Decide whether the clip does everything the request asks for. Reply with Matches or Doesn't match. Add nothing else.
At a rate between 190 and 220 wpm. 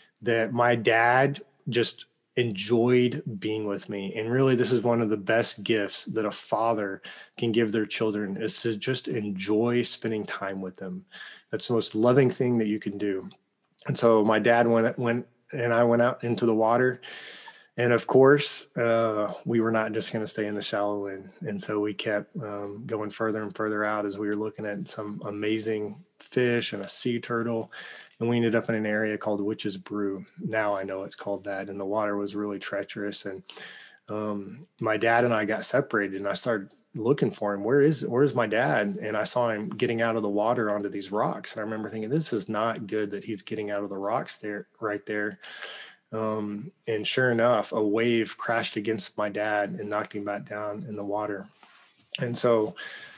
Matches